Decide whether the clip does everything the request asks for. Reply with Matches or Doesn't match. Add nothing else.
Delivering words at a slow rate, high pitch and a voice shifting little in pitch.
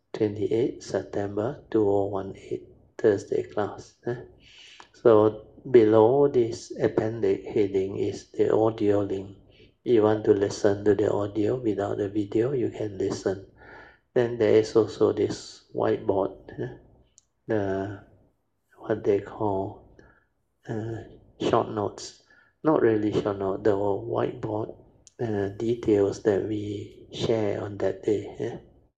Doesn't match